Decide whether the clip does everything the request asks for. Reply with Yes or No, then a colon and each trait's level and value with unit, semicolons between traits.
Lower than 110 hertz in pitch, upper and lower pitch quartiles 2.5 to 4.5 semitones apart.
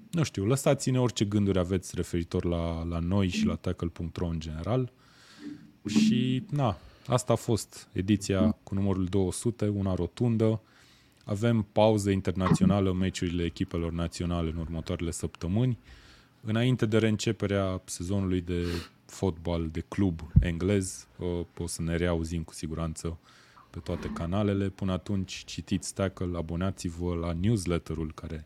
Yes: very low, 95 Hz; average, 4.1 semitones